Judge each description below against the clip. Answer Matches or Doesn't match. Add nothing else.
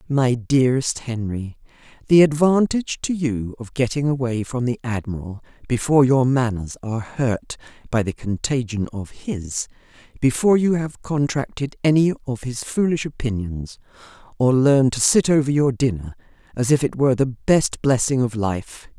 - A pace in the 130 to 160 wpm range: Matches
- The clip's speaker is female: Matches